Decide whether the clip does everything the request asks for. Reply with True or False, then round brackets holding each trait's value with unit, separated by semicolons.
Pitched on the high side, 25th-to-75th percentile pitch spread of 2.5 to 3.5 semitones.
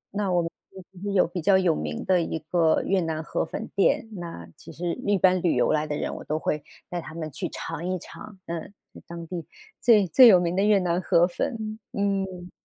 False (180 Hz; 2.8 semitones)